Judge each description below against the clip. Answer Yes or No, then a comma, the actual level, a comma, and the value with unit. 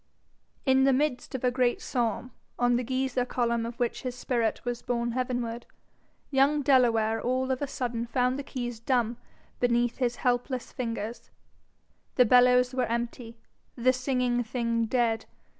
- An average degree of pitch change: No, narrow, 1.4 semitones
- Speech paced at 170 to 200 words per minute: No, average, 155 wpm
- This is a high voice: Yes, high, 245 Hz